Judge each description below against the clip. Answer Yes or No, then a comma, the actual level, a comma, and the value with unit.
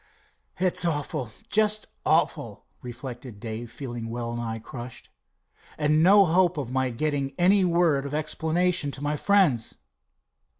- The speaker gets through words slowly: Yes, slow, 130 wpm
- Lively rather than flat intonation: Yes, wide, 6.4 semitones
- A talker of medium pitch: Yes, medium, 145 Hz